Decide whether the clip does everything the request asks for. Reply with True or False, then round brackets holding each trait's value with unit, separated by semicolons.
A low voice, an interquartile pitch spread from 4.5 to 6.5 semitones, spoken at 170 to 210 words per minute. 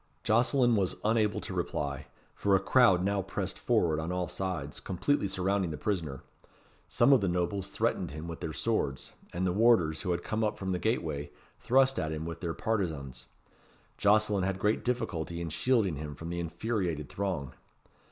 True (90 Hz; 4.9 semitones; 180 wpm)